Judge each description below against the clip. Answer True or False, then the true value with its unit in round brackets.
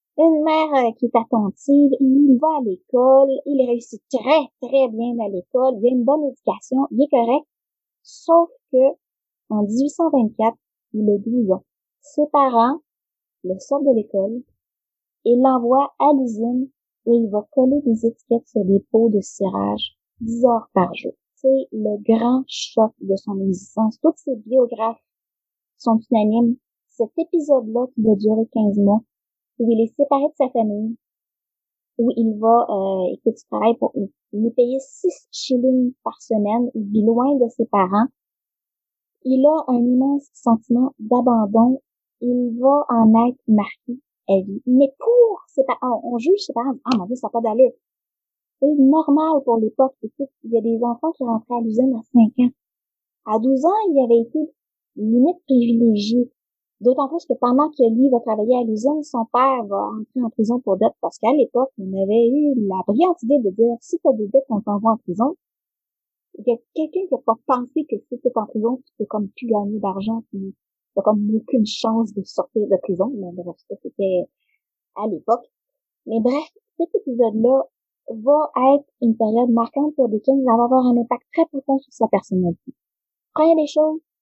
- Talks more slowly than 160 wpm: False (180 wpm)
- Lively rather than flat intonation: False (3.5 semitones)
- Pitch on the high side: True (245 Hz)